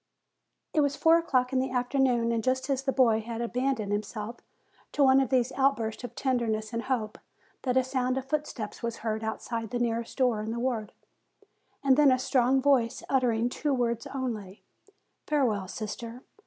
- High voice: Yes, high, 245 Hz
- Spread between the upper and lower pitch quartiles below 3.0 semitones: Yes, narrow, 2.6 semitones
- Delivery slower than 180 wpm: No, average, 185 wpm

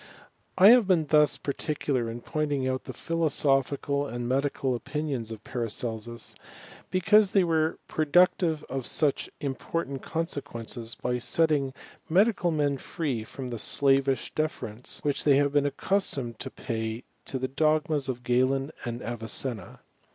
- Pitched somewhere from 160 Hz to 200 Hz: No, medium, 140 Hz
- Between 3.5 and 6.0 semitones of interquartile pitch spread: Yes, average, 4.1 semitones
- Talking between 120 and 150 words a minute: Yes, average, 140 wpm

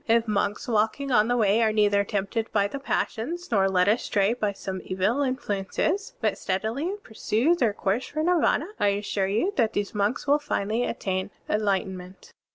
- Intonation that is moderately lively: Yes, average, 3.7 semitones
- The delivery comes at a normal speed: Yes, average, 170 wpm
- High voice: Yes, high, 215 Hz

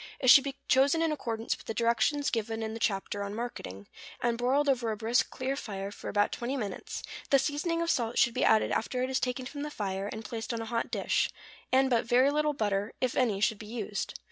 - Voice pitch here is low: No, high, 235 Hz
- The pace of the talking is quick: Yes, fast, 235 wpm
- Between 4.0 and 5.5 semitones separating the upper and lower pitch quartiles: No, average, 3.5 semitones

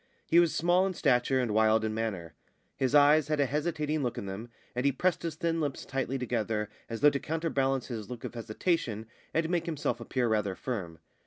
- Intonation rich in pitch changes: Yes, wide, 5.7 semitones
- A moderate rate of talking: No, fast, 210 wpm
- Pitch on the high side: No, low, 130 Hz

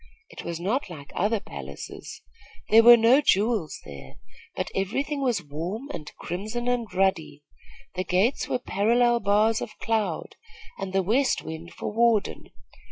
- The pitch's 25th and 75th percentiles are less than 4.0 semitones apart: No, average, 4.7 semitones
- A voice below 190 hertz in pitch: No, high, 210 Hz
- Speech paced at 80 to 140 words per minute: No, average, 155 wpm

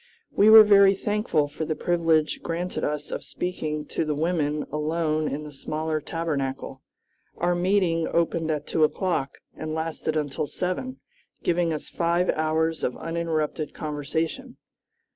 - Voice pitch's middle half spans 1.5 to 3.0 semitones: Yes, narrow, 2.4 semitones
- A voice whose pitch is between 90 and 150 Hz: No, medium, 160 Hz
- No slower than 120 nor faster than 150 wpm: Yes, average, 145 wpm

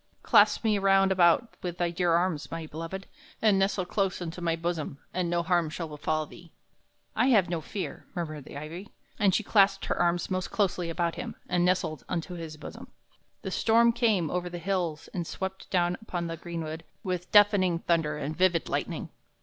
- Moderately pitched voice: Yes, medium, 175 Hz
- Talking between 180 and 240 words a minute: Yes, average, 190 wpm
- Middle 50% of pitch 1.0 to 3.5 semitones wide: Yes, narrow, 2.5 semitones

